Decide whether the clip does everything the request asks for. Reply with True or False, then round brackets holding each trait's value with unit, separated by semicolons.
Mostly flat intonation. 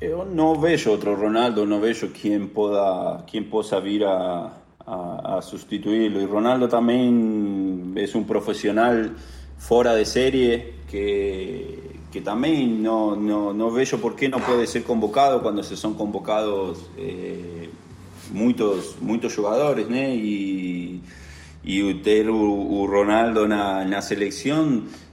False (3.1 semitones)